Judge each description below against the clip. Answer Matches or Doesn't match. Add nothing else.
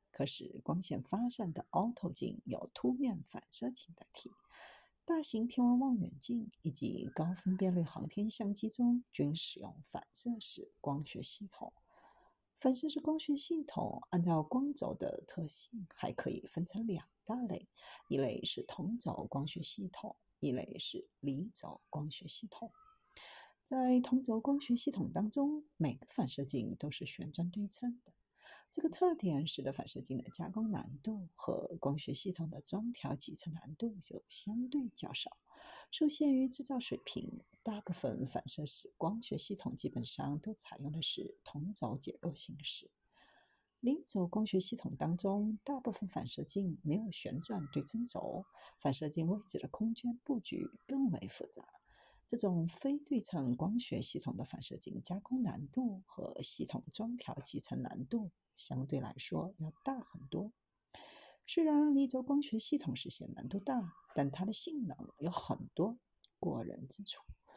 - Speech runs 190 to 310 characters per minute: Matches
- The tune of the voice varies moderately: Doesn't match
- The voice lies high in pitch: Matches